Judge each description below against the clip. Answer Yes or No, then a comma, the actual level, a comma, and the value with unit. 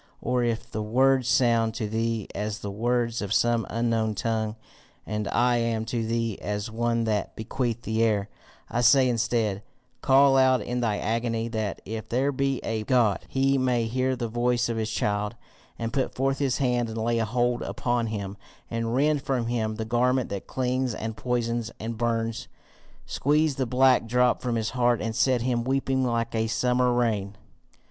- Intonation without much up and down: Yes, narrow, 2.1 semitones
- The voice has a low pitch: Yes, low, 115 Hz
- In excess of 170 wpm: Yes, average, 180 wpm